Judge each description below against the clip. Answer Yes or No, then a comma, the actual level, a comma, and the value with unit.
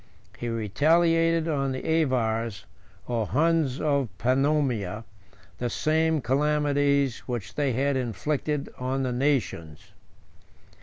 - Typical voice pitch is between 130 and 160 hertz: Yes, low, 135 Hz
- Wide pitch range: No, average, 4.2 semitones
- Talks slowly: Yes, slow, 110 wpm